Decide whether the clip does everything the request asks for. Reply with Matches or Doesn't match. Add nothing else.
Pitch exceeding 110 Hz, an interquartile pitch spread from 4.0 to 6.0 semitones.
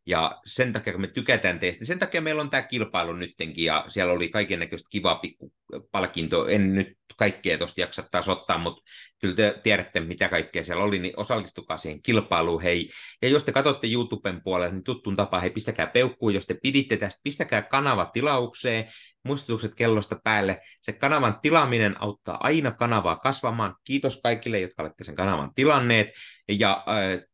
Doesn't match